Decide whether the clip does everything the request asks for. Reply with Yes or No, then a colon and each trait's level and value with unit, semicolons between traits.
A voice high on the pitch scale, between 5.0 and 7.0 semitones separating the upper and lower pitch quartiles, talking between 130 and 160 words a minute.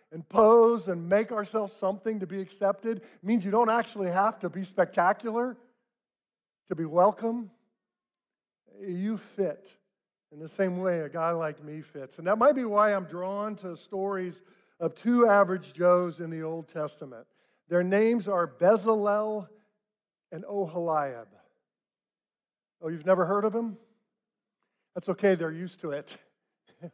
No: high, 195 Hz; average, 3.8 semitones; average, 150 wpm